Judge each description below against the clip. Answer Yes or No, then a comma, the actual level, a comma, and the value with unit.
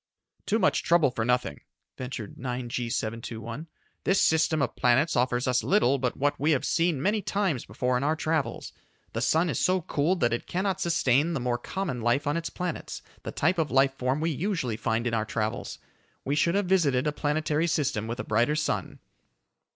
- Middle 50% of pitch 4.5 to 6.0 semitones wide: Yes, average, 5.3 semitones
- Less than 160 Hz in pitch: Yes, medium, 140 Hz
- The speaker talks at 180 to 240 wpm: Yes, average, 195 wpm